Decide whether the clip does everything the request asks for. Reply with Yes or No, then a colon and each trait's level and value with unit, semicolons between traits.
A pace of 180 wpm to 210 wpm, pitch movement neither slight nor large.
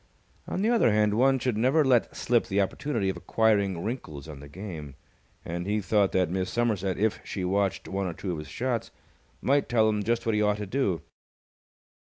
Yes: average, 200 wpm; average, 4.0 semitones